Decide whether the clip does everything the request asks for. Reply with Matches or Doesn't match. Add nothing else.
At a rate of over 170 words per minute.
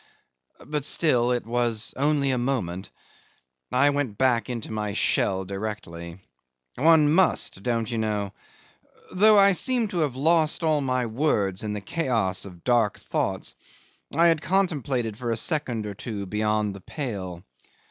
Doesn't match